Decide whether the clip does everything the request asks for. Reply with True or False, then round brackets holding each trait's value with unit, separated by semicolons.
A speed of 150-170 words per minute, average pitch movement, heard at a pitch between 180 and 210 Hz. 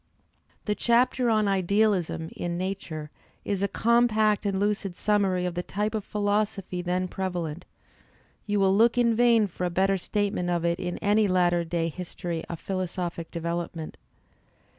True (155 wpm; 3.1 semitones; 190 Hz)